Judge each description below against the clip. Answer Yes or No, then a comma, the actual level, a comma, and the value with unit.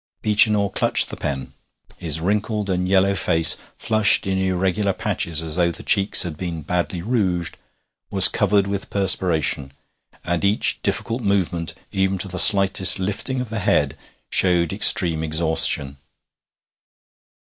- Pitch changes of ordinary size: Yes, average, 3.0 semitones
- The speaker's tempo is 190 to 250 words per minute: No, average, 140 wpm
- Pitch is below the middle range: Yes, very low, 95 Hz